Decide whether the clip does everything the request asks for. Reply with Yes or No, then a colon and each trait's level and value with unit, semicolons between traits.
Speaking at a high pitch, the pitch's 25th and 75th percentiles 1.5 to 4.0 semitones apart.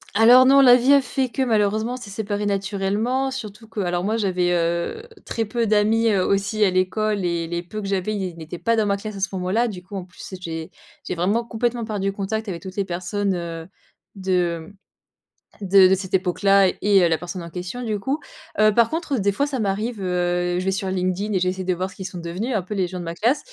Yes: high, 195 Hz; average, 3.3 semitones